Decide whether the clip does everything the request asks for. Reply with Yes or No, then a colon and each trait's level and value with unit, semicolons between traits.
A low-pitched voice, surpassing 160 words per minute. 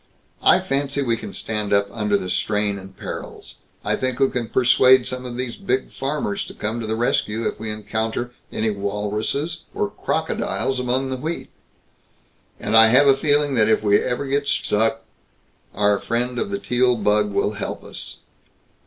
Yes: low, 115 Hz; average, 180 wpm